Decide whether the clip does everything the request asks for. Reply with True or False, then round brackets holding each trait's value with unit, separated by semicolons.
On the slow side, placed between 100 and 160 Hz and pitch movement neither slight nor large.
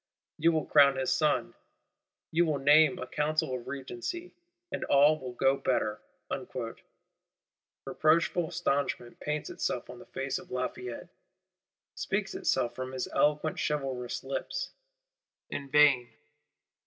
True (125 wpm; 140 Hz; 3.2 semitones)